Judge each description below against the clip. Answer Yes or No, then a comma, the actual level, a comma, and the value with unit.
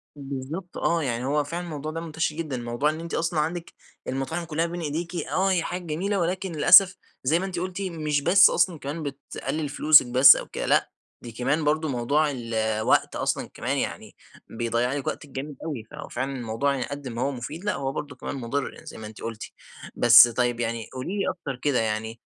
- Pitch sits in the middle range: Yes, medium, 145 Hz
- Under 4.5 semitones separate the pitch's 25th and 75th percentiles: No, average, 4.9 semitones